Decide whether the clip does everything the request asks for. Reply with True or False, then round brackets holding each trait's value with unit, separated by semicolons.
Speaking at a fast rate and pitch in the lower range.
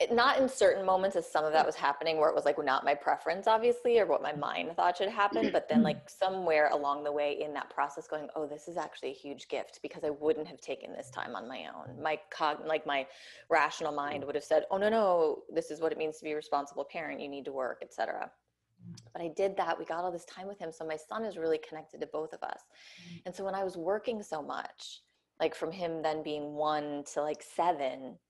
False (250 wpm; 160 Hz)